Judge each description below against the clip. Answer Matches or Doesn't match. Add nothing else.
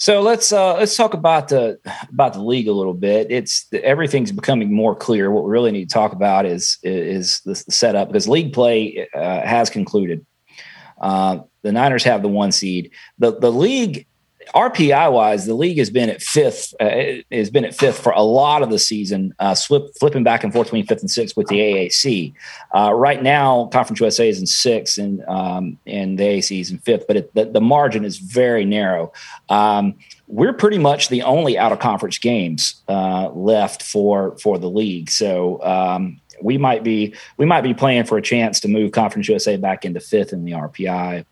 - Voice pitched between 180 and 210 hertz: Doesn't match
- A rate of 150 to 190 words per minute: Doesn't match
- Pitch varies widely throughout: Matches